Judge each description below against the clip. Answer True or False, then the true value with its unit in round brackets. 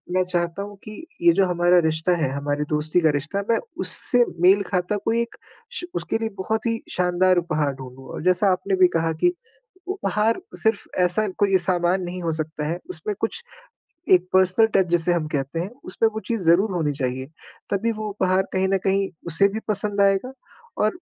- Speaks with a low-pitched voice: False (185 Hz)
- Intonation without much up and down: False (3.7 semitones)